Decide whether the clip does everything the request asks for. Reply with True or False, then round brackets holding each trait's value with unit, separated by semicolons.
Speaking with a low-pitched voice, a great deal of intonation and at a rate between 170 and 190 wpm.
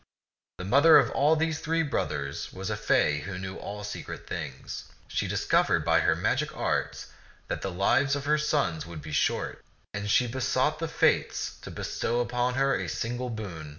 True (120 Hz; 7.4 semitones; 180 wpm)